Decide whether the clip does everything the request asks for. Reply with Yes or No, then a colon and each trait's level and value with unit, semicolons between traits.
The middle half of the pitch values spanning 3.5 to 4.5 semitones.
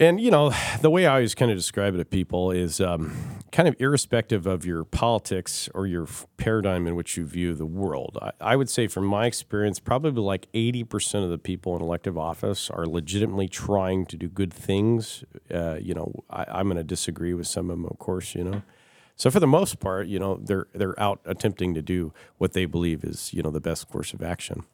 Yes: average, 4.0 semitones